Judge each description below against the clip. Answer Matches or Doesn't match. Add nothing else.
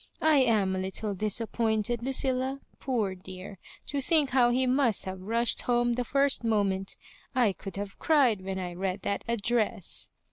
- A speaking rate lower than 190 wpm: Matches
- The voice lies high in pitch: Matches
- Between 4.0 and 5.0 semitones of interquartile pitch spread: Matches